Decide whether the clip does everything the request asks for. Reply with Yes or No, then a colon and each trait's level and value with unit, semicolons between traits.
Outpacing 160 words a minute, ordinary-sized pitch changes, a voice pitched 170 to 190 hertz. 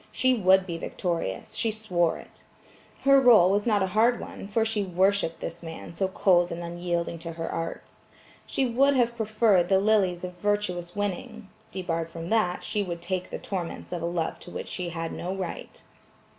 Yes: average, 190 wpm; average, 3.6 semitones; medium, 185 Hz